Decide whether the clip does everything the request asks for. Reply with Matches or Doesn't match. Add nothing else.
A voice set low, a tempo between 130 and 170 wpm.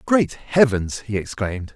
Matches